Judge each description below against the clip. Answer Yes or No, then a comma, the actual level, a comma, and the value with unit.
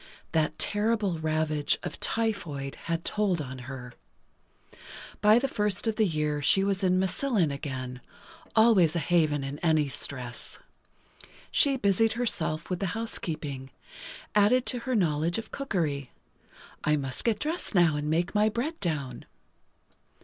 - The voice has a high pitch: No, medium, 170 Hz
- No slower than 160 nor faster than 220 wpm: No, average, 140 wpm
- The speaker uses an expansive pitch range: Yes, wide, 6.4 semitones